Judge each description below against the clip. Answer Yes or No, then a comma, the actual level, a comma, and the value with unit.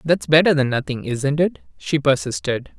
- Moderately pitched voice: Yes, medium, 145 Hz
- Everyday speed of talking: Yes, average, 175 wpm